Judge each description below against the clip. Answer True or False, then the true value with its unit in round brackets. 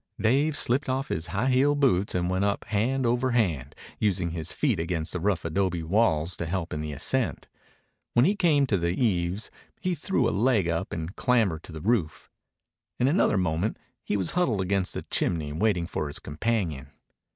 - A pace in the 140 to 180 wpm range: False (190 wpm)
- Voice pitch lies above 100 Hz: False (95 Hz)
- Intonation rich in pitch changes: True (6.5 semitones)